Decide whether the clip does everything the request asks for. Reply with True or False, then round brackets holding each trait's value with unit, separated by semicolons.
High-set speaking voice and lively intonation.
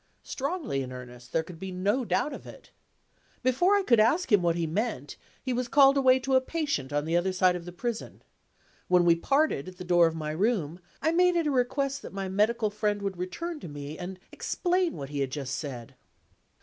True (195 Hz; 8.3 semitones)